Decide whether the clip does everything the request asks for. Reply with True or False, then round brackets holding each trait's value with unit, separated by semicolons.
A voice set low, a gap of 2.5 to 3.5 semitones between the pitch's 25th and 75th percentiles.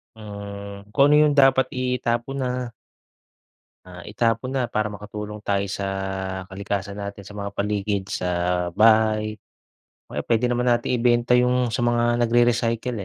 True (115 Hz; 3.0 semitones)